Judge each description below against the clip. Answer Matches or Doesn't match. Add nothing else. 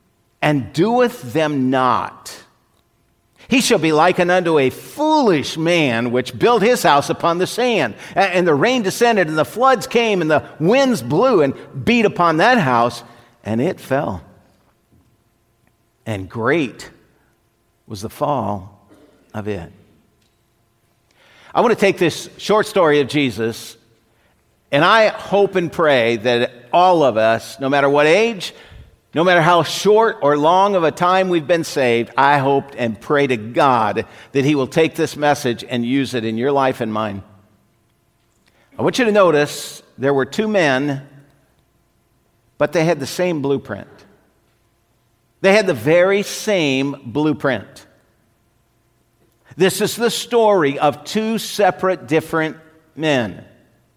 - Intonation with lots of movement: Matches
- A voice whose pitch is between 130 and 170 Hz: Matches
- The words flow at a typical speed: Matches